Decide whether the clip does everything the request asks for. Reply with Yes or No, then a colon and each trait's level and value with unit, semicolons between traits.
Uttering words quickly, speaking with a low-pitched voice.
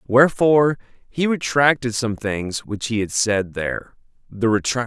No: slow, 135 wpm; low, 120 Hz